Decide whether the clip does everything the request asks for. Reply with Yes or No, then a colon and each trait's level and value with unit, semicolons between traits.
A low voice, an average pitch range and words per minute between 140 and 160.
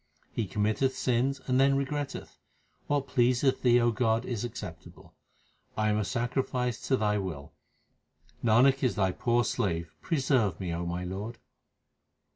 Yes: low, 120 Hz; average, 4.2 semitones; average, 145 wpm